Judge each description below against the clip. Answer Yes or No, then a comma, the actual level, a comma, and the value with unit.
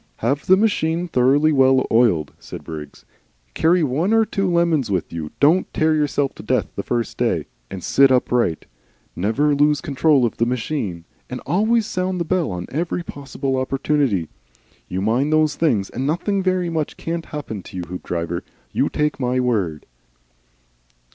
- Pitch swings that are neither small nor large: No, wide, 6.4 semitones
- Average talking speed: Yes, average, 165 wpm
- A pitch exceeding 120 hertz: Yes, medium, 140 Hz